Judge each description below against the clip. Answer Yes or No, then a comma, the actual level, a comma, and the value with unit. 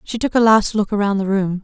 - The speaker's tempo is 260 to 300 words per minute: Yes, fast, 295 wpm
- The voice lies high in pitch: Yes, high, 205 Hz